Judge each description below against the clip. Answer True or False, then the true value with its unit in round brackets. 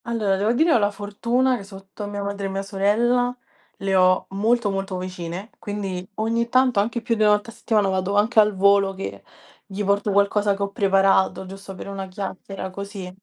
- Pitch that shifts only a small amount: True (1.9 semitones)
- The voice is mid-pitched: False (200 Hz)